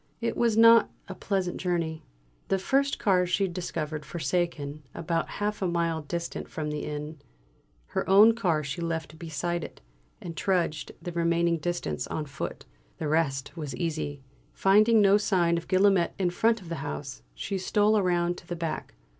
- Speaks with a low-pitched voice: No, medium, 170 Hz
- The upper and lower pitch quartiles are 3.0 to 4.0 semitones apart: Yes, average, 3.5 semitones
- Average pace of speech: Yes, average, 170 wpm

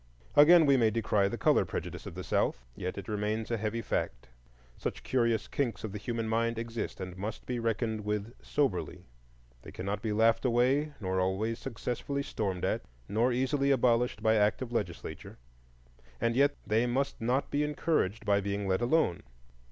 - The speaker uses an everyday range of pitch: Yes, average, 3.4 semitones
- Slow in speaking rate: No, average, 175 wpm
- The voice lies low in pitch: Yes, low, 115 Hz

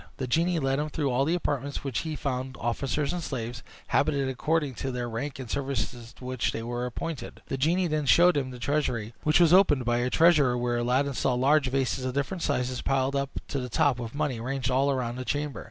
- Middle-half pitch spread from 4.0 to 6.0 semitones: No, average, 3.0 semitones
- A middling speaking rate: No, fast, 230 wpm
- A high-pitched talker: No, low, 135 Hz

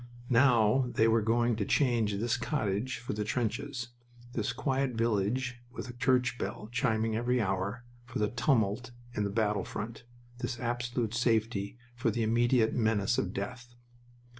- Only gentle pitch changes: Yes, narrow, 2.3 semitones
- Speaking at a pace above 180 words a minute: No, average, 155 wpm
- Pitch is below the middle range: Yes, low, 115 Hz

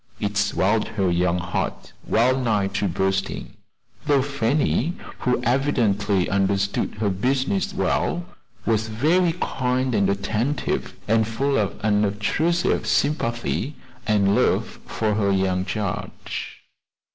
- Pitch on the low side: Yes, low, 110 Hz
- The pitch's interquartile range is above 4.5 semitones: Yes, average, 4.9 semitones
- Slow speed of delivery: Yes, slow, 110 wpm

